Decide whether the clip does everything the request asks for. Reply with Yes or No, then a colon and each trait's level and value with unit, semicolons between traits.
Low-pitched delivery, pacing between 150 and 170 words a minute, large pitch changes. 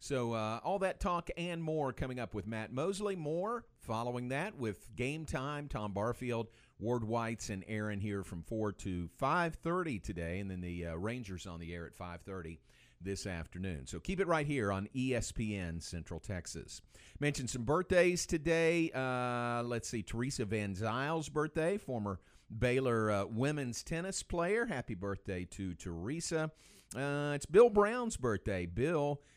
Yes: low, 120 Hz; average, 160 wpm; wide, 7.1 semitones